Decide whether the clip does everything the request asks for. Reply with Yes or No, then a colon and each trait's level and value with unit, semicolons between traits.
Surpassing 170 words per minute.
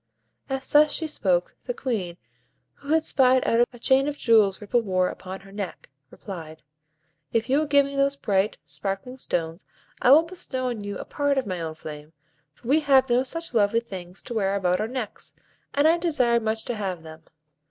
Yes: average, 200 wpm